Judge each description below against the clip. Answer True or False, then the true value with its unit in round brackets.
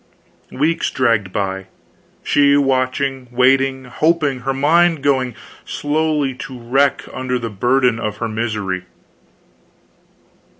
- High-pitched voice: False (130 Hz)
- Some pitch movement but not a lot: True (3.2 semitones)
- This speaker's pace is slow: True (110 wpm)